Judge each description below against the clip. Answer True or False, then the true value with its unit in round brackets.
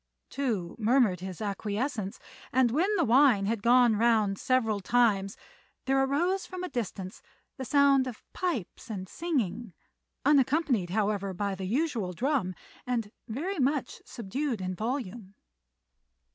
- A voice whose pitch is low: False (235 Hz)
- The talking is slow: True (130 wpm)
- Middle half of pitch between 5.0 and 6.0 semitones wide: True (5.5 semitones)